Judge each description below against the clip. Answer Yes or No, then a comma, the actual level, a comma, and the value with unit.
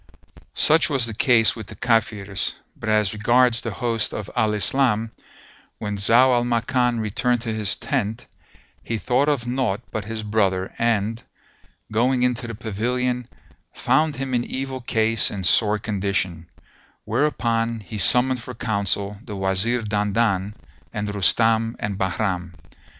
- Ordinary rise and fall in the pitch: Yes, average, 3.0 semitones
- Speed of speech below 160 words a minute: Yes, average, 145 wpm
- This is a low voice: Yes, low, 110 Hz